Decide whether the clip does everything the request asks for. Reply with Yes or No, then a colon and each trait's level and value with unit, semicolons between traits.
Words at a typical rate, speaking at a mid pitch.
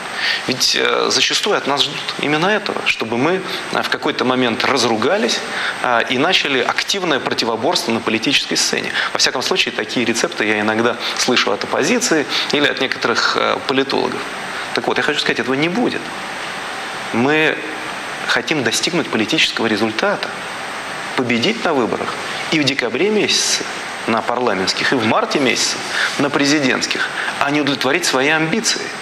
No: average, 140 wpm; low, 130 Hz